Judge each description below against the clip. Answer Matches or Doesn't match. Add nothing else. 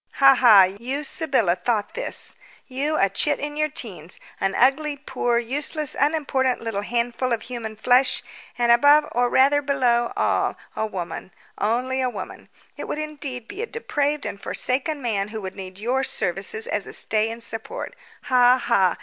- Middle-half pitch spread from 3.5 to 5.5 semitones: Matches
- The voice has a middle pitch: Doesn't match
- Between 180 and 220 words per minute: Doesn't match